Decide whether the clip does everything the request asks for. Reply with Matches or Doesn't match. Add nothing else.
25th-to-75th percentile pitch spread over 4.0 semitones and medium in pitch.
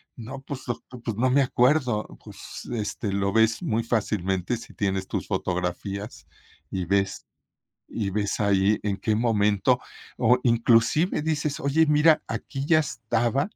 Doesn't match